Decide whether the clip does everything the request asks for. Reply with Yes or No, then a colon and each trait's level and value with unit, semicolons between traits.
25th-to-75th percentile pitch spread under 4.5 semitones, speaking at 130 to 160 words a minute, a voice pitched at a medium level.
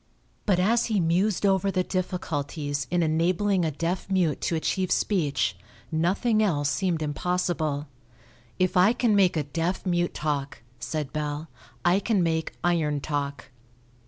Yes: average, 3.8 semitones; average, 145 wpm; medium, 175 Hz